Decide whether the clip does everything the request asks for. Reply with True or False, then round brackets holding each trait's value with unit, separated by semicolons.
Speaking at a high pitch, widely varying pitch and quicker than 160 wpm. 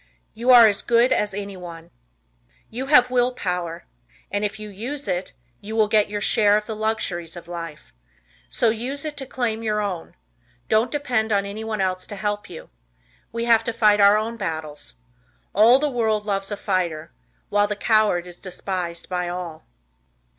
False (210 Hz; 3.6 semitones; 175 wpm)